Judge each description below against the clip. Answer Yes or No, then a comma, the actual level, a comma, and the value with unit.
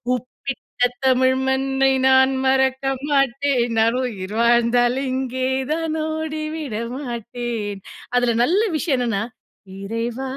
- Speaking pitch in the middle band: No, very high, 260 Hz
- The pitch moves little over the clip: Yes, narrow, 2.2 semitones